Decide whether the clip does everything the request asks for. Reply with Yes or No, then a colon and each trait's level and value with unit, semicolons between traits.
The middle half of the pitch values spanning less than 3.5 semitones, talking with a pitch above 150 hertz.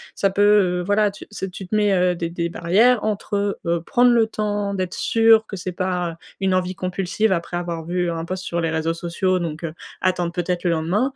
Yes: average, 2.9 semitones; medium, 185 Hz